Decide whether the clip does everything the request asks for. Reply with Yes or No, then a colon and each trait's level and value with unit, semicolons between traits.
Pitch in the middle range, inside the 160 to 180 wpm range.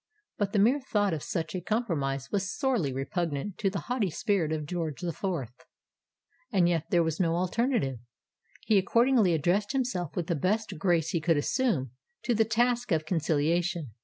Yes: medium, 180 Hz; average, 175 wpm